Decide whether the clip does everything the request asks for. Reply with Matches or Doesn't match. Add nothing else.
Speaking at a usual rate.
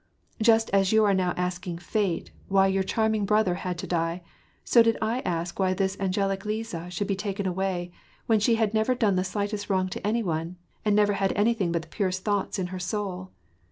Doesn't match